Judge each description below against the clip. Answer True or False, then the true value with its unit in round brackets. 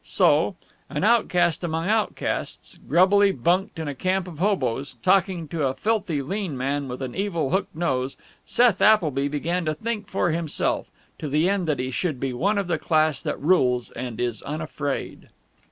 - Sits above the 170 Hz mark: False (160 Hz)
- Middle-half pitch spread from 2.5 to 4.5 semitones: False (5.4 semitones)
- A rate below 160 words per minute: False (175 wpm)